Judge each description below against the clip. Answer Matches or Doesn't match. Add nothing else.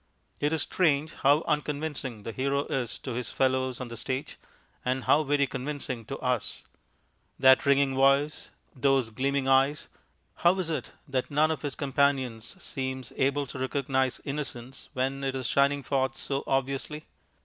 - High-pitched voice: Doesn't match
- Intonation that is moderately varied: Doesn't match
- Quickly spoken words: Doesn't match